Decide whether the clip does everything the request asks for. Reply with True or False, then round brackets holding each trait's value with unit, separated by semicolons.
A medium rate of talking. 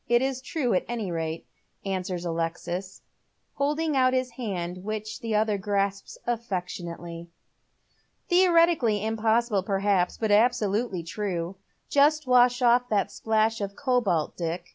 False (120 wpm)